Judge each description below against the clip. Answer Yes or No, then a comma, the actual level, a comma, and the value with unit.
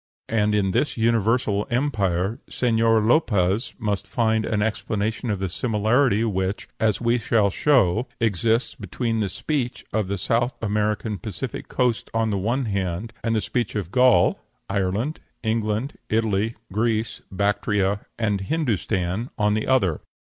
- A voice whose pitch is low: Yes, low, 110 Hz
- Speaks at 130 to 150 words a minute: Yes, average, 140 wpm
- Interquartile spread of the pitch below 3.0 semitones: Yes, narrow, 2.6 semitones